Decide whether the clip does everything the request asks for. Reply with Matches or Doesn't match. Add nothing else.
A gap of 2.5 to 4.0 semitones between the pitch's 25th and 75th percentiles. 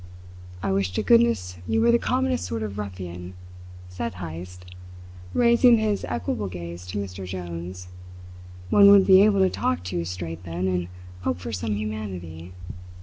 Doesn't match